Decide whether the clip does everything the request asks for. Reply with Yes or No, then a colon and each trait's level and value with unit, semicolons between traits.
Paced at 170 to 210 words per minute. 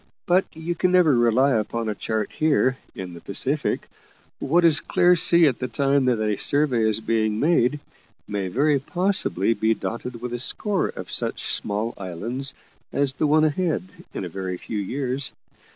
Yes: average, 175 wpm